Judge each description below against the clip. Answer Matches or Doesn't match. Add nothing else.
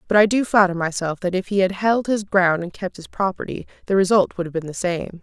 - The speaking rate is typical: Doesn't match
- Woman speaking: Matches